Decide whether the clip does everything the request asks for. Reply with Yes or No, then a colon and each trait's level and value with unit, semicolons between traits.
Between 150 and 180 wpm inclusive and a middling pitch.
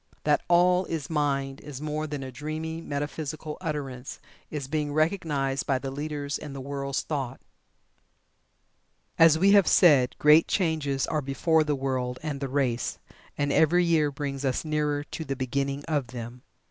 Yes: average, 160 wpm; medium, 145 Hz